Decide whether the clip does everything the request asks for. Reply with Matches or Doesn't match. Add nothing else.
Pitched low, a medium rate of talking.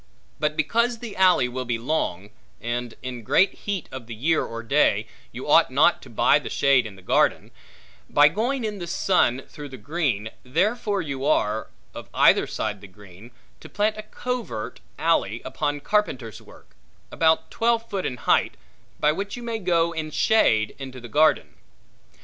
Doesn't match